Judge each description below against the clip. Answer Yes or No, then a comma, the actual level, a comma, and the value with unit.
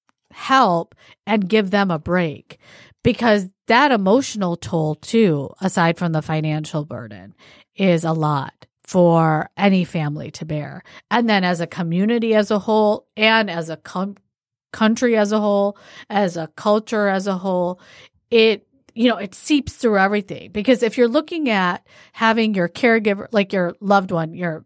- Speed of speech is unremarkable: Yes, average, 160 wpm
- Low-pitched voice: No, high, 195 Hz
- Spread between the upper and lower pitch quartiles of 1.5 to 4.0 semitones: No, average, 4.7 semitones